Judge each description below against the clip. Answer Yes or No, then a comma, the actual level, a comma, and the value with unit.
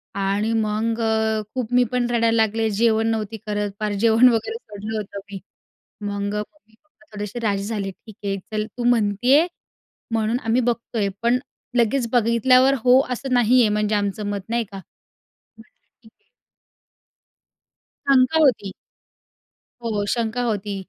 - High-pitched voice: Yes, high, 225 Hz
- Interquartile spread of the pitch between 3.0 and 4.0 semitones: No, narrow, 2.6 semitones